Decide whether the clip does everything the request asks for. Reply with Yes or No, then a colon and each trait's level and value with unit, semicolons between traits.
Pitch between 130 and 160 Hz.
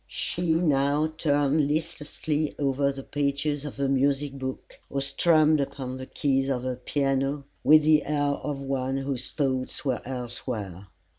Yes: medium, 140 Hz